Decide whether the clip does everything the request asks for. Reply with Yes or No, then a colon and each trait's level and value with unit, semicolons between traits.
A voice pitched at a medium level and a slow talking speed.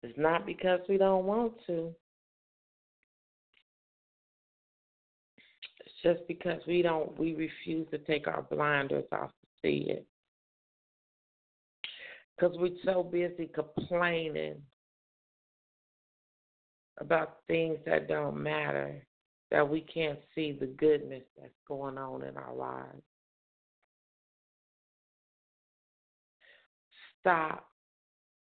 Yes: medium, 155 Hz; slow, 95 wpm